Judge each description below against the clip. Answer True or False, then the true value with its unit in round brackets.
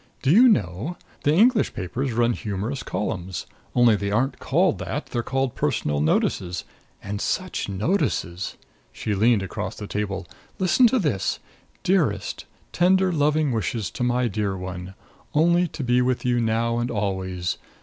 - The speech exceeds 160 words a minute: False (150 wpm)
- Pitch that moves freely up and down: True (7.1 semitones)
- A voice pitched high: False (115 Hz)